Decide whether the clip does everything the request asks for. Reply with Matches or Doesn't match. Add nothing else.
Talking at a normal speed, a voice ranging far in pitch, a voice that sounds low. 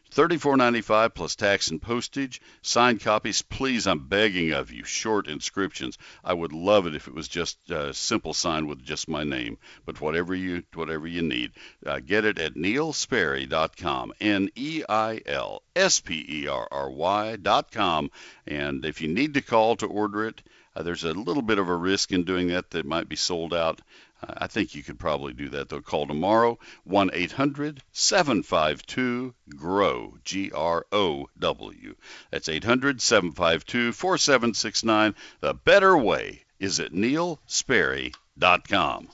Matches